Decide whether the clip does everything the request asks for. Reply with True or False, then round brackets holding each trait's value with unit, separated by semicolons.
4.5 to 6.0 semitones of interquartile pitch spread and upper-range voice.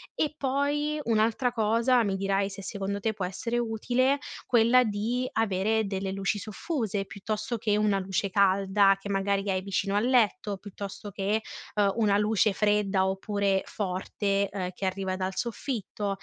False (2.4 semitones; 205 Hz)